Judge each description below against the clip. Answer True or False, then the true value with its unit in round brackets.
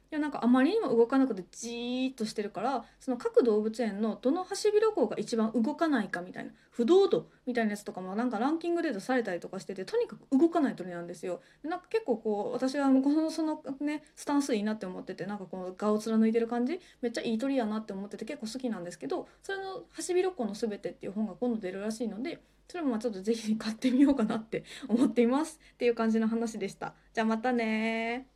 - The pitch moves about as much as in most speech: True (3.8 semitones)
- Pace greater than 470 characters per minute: True (490 characters per minute)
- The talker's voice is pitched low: False (235 Hz)